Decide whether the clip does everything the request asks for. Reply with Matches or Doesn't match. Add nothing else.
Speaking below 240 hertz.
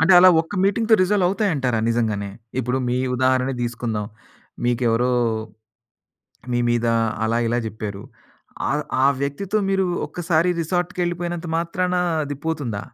Matches